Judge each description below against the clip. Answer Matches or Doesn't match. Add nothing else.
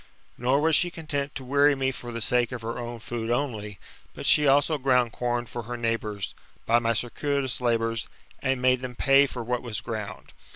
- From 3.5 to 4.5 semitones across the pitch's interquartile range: Doesn't match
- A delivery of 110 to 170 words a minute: Doesn't match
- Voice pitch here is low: Matches